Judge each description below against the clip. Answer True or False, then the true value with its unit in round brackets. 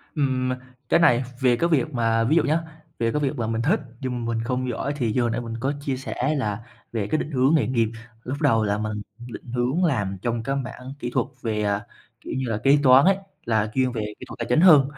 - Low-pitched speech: True (125 Hz)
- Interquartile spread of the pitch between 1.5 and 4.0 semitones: True (3.3 semitones)